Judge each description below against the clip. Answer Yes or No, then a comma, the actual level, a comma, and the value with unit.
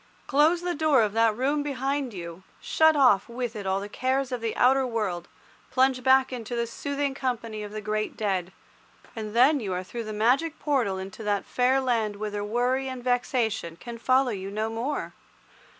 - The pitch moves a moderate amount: Yes, average, 3.9 semitones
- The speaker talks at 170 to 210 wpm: Yes, average, 190 wpm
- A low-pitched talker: No, high, 240 Hz